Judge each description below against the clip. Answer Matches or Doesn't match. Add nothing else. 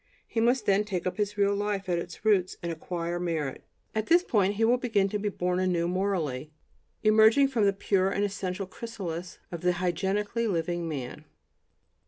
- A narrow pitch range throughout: Doesn't match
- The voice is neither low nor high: Doesn't match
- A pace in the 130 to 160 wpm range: Doesn't match